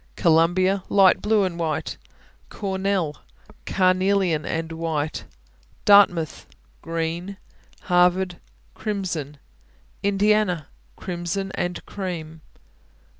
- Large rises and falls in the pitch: No, average, 3.1 semitones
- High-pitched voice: No, medium, 180 Hz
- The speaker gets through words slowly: Yes, slow, 75 wpm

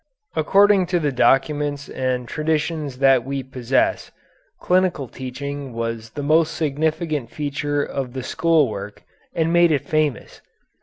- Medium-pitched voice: Yes, medium, 145 Hz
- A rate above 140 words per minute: No, slow, 135 wpm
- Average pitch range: Yes, average, 3.3 semitones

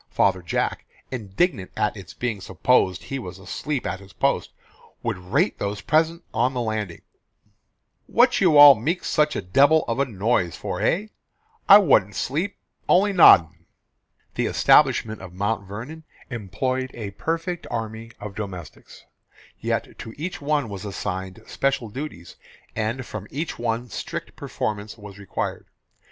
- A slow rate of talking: No, average, 145 wpm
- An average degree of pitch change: No, wide, 6.8 semitones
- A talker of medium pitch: No, low, 115 Hz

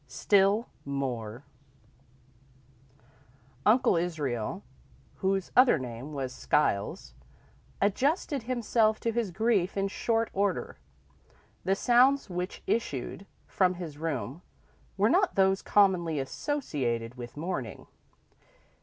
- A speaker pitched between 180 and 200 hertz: Yes, medium, 185 Hz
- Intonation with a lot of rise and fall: Yes, wide, 8.2 semitones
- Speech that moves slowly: Yes, slow, 100 wpm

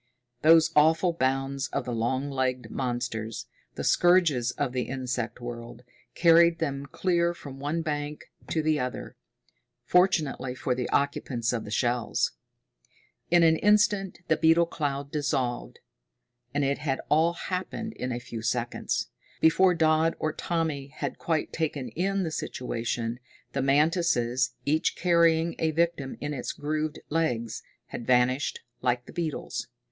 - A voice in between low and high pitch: Yes, medium, 145 Hz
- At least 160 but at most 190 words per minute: No, average, 140 wpm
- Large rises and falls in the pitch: No, average, 4.6 semitones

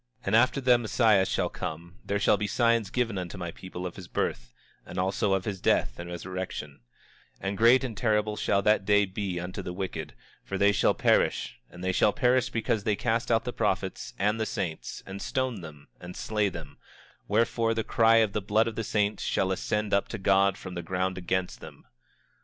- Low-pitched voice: Yes, low, 100 Hz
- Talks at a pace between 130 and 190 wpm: No, fast, 205 wpm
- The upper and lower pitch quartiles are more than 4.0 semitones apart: No, average, 3.3 semitones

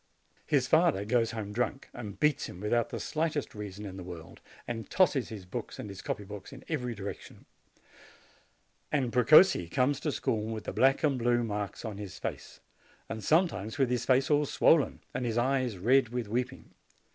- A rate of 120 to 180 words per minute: No, average, 190 wpm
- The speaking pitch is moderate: No, low, 120 Hz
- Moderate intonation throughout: Yes, average, 4.5 semitones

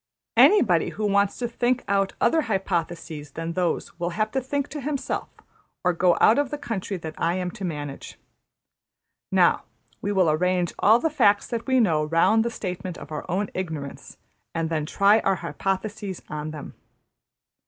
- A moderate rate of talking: Yes, average, 175 wpm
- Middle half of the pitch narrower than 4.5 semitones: No, average, 5.0 semitones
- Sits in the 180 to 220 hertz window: Yes, high, 190 Hz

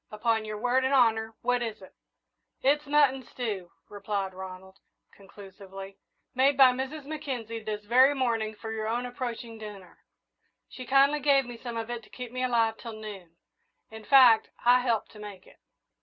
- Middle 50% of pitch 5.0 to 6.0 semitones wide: No, average, 3.4 semitones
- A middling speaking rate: Yes, average, 170 wpm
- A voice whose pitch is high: Yes, high, 230 Hz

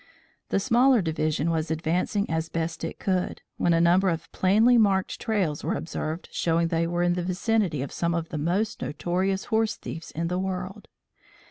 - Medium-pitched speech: Yes, medium, 175 Hz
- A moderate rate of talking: Yes, average, 185 wpm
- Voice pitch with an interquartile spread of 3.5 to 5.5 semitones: No, average, 3.0 semitones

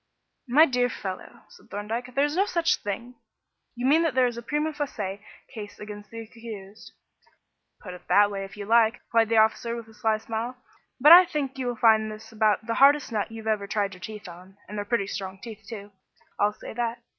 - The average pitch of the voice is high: Yes, high, 225 Hz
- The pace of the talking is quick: Yes, fast, 215 wpm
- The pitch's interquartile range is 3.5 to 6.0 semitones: No, average, 3.0 semitones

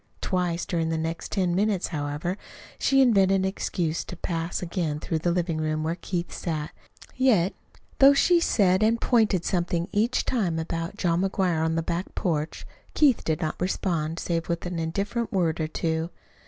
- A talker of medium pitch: Yes, medium, 175 Hz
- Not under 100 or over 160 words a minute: No, average, 175 wpm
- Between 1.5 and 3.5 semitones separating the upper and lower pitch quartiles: Yes, average, 3.0 semitones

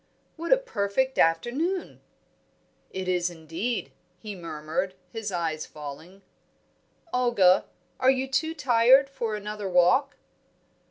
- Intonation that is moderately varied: No, wide, 6.8 semitones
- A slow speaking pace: Yes, slow, 110 wpm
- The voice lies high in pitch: Yes, high, 210 Hz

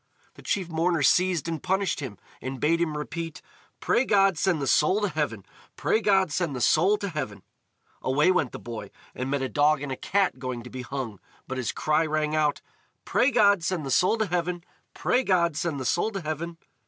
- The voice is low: No, medium, 160 Hz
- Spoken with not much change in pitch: No, average, 5.1 semitones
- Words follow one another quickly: Yes, fast, 210 wpm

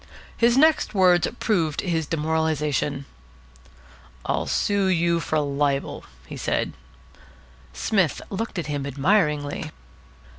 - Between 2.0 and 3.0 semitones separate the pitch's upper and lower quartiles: No, average, 4.6 semitones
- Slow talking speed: Yes, slow, 105 wpm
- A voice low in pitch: No, medium, 160 Hz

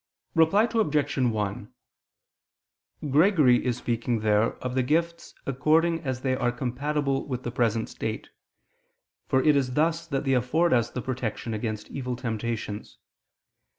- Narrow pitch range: No, average, 4.1 semitones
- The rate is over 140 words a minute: No, slow, 135 wpm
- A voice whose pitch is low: Yes, low, 130 Hz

